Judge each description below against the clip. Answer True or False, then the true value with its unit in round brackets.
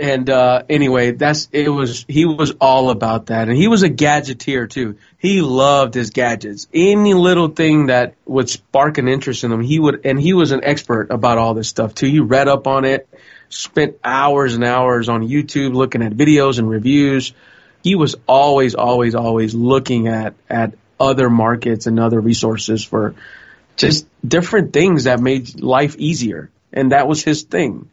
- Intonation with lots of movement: False (3.9 semitones)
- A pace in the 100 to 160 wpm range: False (185 wpm)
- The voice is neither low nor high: False (130 Hz)